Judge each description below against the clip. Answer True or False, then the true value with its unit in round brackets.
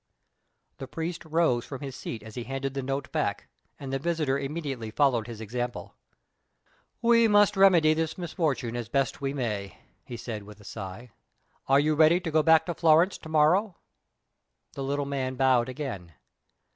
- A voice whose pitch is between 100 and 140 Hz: True (135 Hz)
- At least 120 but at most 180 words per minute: True (170 wpm)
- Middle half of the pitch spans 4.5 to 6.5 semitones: True (4.8 semitones)